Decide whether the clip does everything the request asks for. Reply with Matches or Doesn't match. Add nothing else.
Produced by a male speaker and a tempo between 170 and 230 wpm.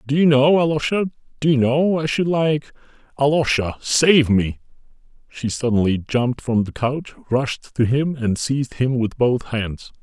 Doesn't match